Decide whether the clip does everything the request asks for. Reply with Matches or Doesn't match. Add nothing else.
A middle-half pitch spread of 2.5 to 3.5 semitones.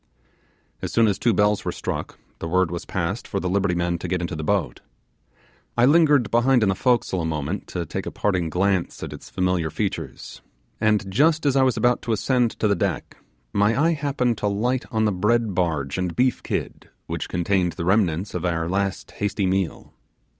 Doesn't match